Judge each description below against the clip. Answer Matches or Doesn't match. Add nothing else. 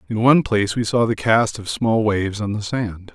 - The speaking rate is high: Matches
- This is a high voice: Doesn't match